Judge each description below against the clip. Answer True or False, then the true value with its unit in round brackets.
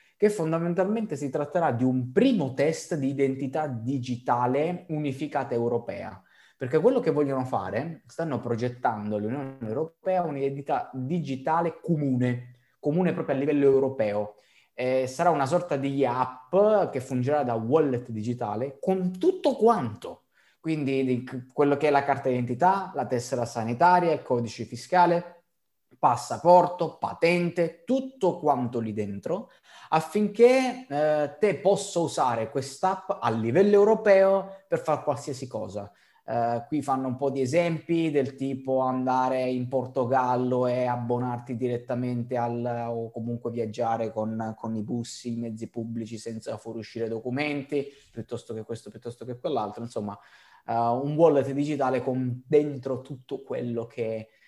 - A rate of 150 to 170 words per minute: False (135 wpm)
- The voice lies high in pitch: False (135 Hz)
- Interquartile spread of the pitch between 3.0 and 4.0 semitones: False (5.1 semitones)